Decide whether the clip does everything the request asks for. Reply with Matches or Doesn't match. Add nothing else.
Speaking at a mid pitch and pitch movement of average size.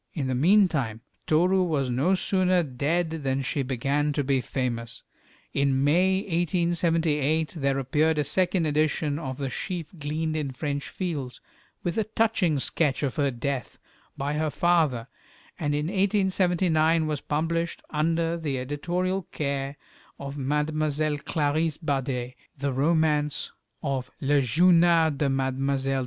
Matches